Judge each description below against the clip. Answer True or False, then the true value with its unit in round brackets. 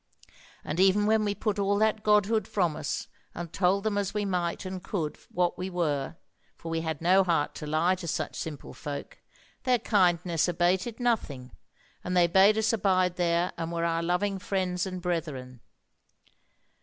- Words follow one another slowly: False (175 wpm)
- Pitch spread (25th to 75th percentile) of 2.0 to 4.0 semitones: True (3.2 semitones)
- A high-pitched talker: False (180 Hz)